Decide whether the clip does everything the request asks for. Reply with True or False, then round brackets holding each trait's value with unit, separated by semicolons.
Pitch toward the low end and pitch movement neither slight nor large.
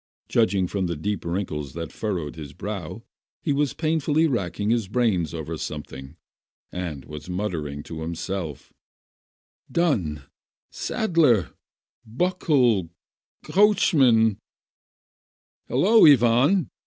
False (100 Hz; 9.0 semitones)